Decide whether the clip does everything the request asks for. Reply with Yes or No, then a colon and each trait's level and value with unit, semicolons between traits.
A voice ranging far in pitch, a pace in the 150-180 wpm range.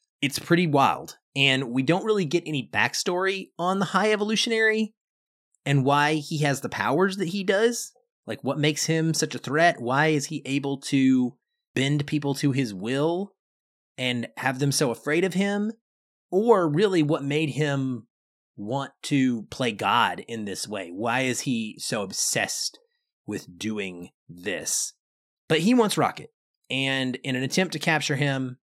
Yes: wide, 6.0 semitones; average, 165 wpm